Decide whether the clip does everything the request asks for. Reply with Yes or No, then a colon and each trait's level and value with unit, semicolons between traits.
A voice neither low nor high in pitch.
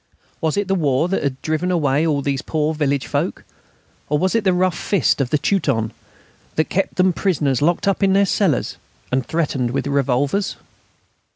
Yes: medium, 155 Hz